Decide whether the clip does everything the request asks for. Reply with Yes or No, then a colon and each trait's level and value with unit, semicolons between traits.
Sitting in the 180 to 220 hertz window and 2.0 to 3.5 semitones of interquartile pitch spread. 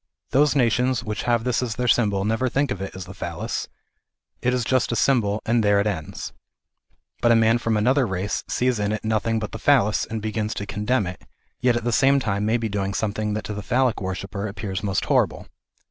No: low, 110 Hz; average, 3.0 semitones